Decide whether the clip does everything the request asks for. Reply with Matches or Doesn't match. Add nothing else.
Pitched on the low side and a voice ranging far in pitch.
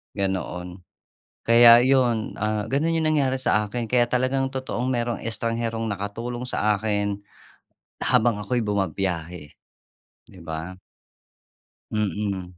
Doesn't match